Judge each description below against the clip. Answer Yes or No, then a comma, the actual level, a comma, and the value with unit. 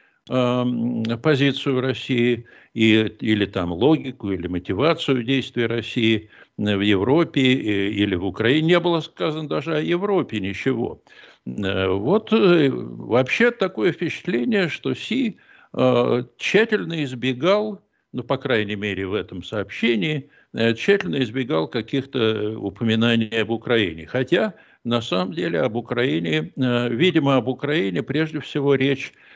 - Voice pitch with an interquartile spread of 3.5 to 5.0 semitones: No, wide, 5.4 semitones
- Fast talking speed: No, average, 115 wpm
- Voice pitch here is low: Yes, low, 125 Hz